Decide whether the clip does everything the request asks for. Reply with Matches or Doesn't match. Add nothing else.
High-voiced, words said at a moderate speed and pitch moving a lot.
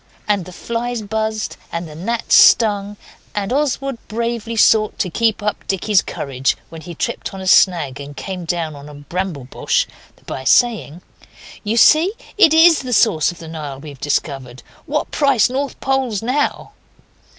Matches